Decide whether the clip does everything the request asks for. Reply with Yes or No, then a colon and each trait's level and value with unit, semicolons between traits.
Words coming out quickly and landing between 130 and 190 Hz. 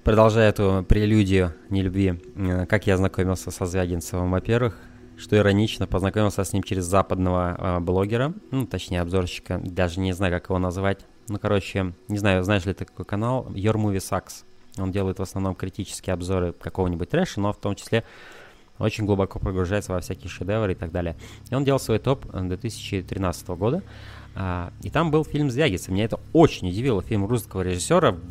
No: fast, 165 wpm; very low, 95 Hz